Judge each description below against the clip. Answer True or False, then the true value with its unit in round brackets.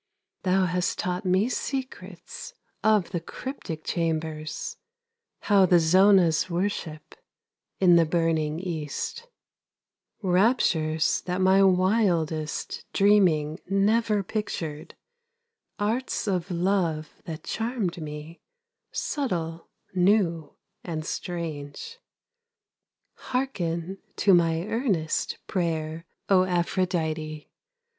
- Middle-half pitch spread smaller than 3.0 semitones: False (3.6 semitones)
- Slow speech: True (90 wpm)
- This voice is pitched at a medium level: True (180 Hz)